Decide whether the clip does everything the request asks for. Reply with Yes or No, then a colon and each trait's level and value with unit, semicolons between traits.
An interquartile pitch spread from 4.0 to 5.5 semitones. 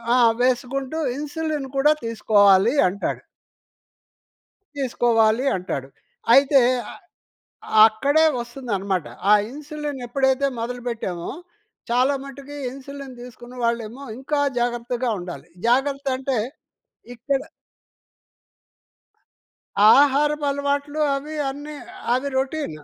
No: average, 3.3 semitones